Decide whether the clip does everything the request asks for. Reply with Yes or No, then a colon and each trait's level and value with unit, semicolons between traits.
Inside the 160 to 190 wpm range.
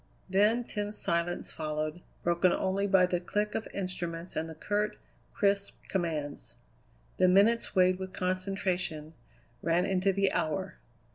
No: slow, 135 wpm